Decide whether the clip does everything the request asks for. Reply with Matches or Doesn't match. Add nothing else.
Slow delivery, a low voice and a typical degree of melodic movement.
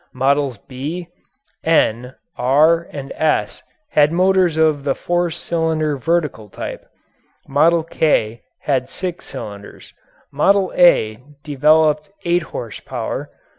Doesn't match